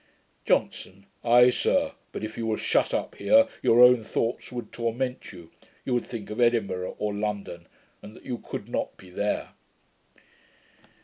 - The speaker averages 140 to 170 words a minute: Yes, average, 165 wpm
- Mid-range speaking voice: No, low, 115 Hz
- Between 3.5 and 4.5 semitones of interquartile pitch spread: No, average, 3.1 semitones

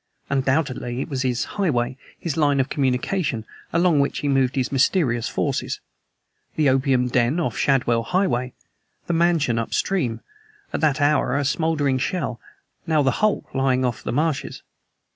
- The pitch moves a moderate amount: Yes, average, 3.9 semitones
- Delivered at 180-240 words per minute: No, average, 150 wpm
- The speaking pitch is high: No, low, 135 Hz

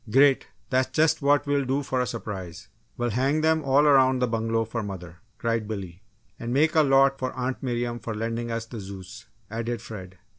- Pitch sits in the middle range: No, low, 120 Hz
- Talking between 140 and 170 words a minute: No, average, 195 wpm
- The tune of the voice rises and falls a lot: No, average, 3.4 semitones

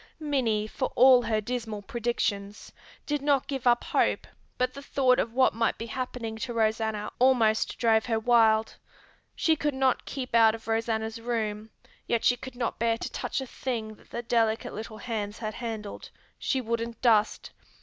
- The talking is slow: No, average, 175 wpm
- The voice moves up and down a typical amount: No, narrow, 2.3 semitones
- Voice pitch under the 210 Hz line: No, high, 230 Hz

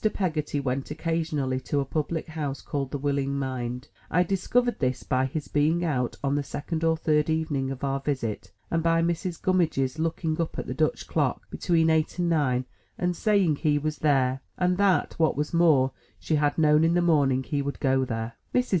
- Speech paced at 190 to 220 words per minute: Yes, average, 200 wpm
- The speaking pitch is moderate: Yes, medium, 150 Hz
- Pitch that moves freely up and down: No, average, 3.5 semitones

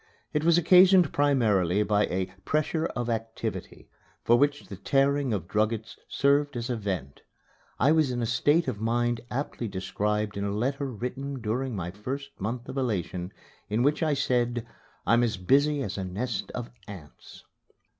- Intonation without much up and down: No, average, 5.1 semitones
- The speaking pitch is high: No, low, 120 Hz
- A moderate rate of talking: Yes, average, 165 wpm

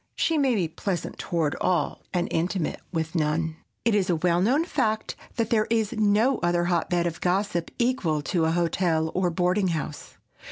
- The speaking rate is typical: Yes, average, 185 wpm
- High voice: No, medium, 180 Hz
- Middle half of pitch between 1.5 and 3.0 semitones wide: No, average, 4.5 semitones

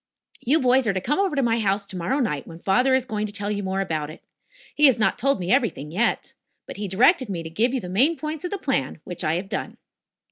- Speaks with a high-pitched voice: Yes, high, 210 Hz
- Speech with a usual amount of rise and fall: No, wide, 6.0 semitones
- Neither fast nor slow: No, fast, 260 wpm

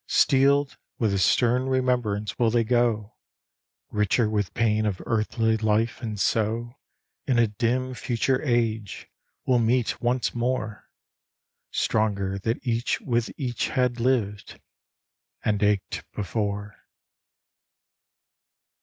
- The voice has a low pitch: Yes, low, 115 Hz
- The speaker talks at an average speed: No, slow, 110 wpm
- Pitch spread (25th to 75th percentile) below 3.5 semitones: Yes, average, 2.7 semitones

